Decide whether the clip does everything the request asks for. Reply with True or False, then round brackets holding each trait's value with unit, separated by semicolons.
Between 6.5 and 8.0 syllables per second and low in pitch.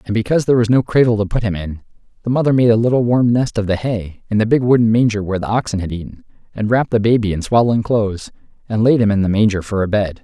True (6.9 syllables/s; 110 Hz)